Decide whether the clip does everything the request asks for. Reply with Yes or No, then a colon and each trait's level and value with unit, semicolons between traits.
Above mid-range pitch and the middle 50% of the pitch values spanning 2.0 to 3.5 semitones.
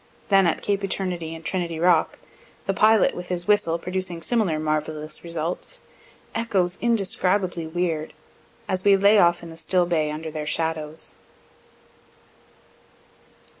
No: medium, 175 Hz; average, 3.2 semitones